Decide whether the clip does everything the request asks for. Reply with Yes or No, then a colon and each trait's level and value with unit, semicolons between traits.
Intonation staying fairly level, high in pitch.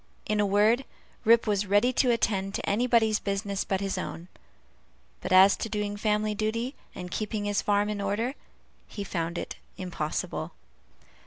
Yes: narrow, 1.8 semitones; high, 205 Hz